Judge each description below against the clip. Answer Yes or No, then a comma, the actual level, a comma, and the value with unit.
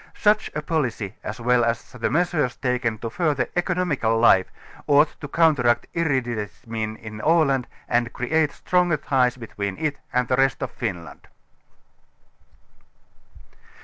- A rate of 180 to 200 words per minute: No, slow, 135 wpm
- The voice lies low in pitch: Yes, low, 125 Hz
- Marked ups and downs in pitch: No, average, 5.0 semitones